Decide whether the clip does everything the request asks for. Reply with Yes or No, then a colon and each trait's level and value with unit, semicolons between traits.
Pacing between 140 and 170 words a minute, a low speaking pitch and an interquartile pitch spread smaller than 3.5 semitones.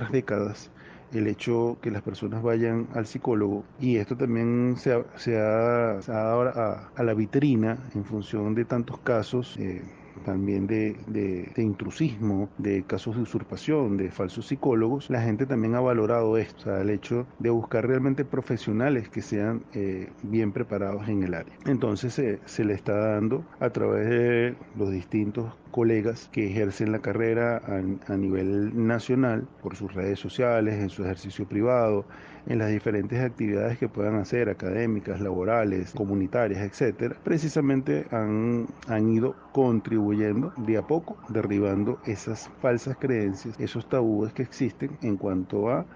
Yes: average, 155 wpm; low, 110 Hz; average, 2.9 semitones